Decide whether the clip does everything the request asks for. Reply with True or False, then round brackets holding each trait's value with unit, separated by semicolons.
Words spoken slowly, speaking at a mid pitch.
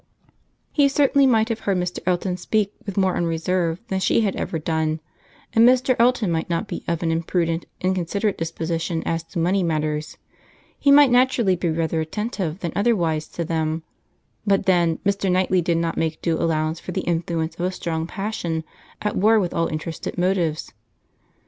False (175 wpm; 175 Hz)